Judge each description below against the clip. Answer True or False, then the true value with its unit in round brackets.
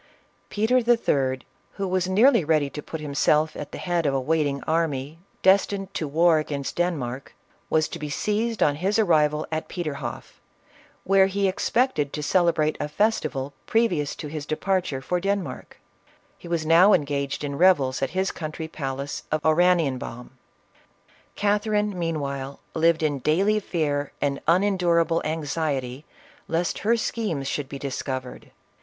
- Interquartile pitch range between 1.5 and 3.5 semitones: False (4.6 semitones)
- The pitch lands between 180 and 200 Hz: False (160 Hz)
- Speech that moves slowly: False (150 wpm)